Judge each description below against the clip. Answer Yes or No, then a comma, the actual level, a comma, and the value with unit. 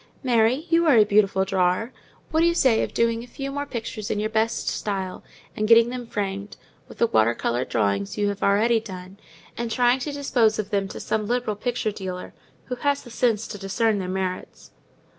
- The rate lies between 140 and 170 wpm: No, fast, 205 wpm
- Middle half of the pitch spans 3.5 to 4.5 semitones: Yes, average, 3.8 semitones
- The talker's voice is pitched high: Yes, high, 220 Hz